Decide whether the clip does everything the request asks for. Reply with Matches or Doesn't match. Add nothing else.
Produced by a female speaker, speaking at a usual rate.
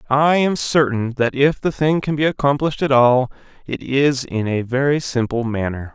Doesn't match